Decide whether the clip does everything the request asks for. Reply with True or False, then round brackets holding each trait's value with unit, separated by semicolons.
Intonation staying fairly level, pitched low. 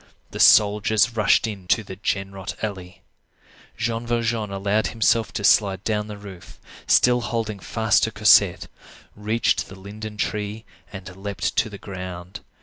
True (2.2 semitones; 105 Hz)